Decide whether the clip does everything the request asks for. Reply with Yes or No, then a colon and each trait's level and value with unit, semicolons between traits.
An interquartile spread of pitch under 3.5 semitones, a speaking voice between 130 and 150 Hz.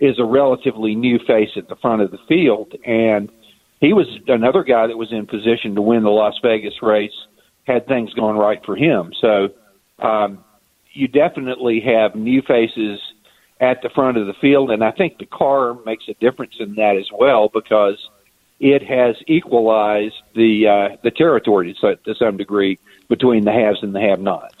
No: average, 3.0 semitones; low, 110 Hz